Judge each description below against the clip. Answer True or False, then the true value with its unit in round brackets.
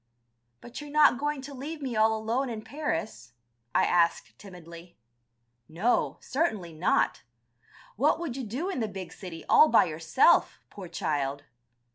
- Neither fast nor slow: True (150 wpm)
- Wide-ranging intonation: True (8.4 semitones)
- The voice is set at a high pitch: True (220 Hz)